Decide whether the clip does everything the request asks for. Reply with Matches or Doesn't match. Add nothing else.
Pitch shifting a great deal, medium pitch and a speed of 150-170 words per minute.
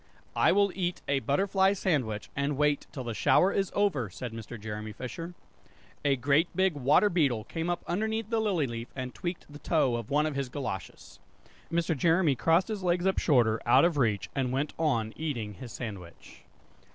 Doesn't match